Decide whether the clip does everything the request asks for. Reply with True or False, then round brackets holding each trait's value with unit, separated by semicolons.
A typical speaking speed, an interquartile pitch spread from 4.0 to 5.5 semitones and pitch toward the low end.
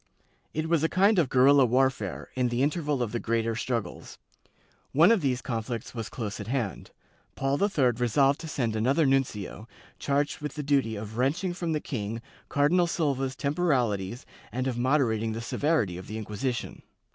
True (170 wpm; 4.4 semitones; 130 Hz)